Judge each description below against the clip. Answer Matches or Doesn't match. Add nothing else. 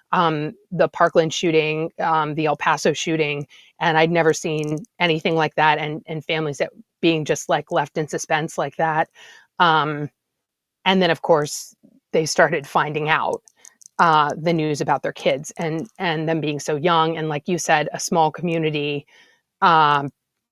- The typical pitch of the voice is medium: Matches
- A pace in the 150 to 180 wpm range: Matches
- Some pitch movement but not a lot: Doesn't match